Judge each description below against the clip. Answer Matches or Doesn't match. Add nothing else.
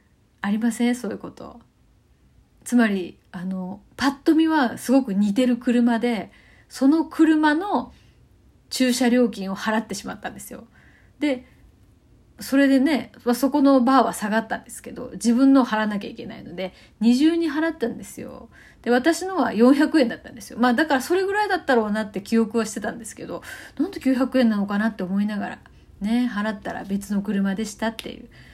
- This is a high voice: Matches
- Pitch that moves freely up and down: Doesn't match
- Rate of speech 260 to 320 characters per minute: Doesn't match